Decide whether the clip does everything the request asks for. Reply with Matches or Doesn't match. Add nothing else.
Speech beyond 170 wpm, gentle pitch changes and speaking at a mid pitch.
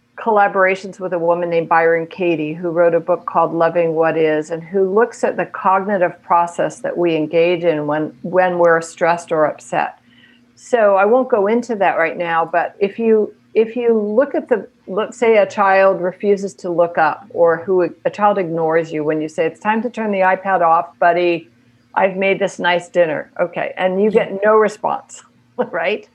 Doesn't match